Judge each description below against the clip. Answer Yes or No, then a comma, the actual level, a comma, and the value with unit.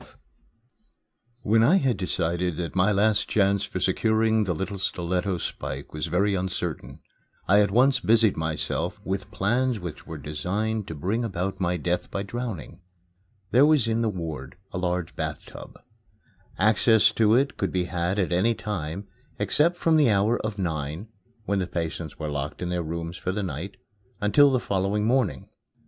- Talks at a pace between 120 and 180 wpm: Yes, average, 170 wpm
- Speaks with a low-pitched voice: Yes, very low, 95 Hz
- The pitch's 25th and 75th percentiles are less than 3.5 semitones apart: No, average, 4.0 semitones